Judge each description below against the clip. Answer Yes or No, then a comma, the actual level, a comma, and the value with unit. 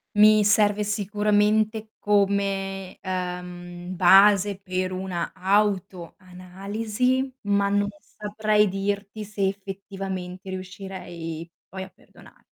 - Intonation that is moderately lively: No, narrow, 2.0 semitones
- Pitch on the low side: No, high, 195 Hz